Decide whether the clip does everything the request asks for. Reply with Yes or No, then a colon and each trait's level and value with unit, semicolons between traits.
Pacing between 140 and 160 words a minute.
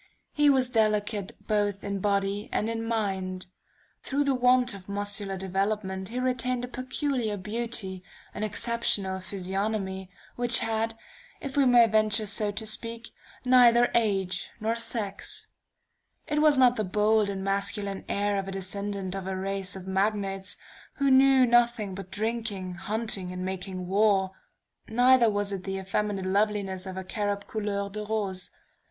Yes: average, 150 wpm